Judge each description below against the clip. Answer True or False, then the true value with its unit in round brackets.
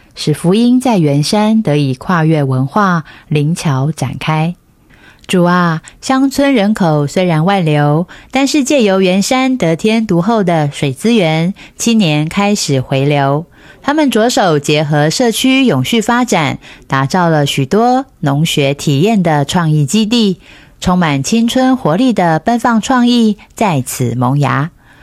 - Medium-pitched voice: True (175 Hz)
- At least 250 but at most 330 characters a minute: False (210 characters per minute)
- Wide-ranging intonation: True (7.4 semitones)